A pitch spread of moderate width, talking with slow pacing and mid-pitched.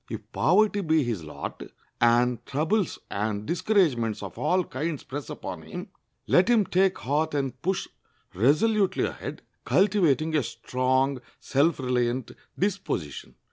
No: wide, 6.9 semitones; slow, 130 wpm; medium, 150 Hz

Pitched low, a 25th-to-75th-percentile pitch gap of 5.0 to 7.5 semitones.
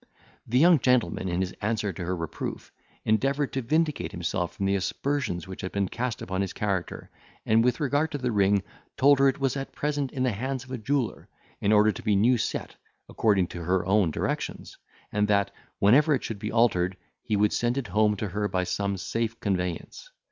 Yes: low, 110 Hz; average, 5.3 semitones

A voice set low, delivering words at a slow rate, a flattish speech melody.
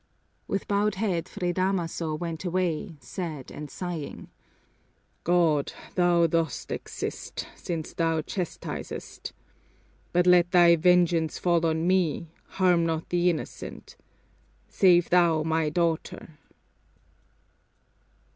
No: medium, 170 Hz; slow, 105 wpm; narrow, 1.8 semitones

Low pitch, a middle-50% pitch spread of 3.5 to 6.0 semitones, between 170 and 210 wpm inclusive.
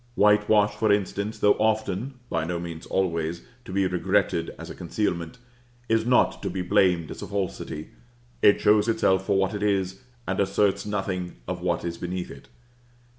No: very low, 95 Hz; average, 2.7 semitones; average, 175 wpm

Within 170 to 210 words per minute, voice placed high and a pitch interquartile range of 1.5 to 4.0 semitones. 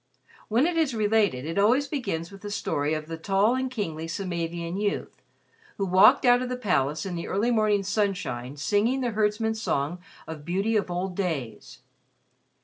No: average, 175 wpm; high, 200 Hz; average, 5.0 semitones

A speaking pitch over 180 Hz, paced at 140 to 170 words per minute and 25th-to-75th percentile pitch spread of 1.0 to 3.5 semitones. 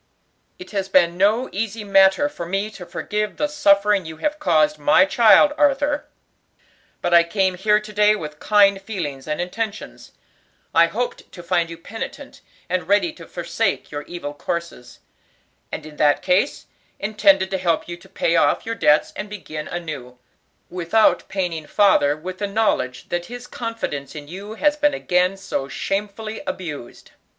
No: high, 190 Hz; average, 165 wpm; average, 4.3 semitones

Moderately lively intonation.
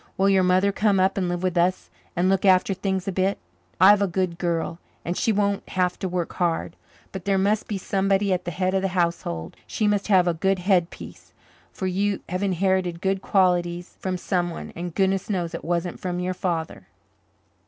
No: narrow, 1.7 semitones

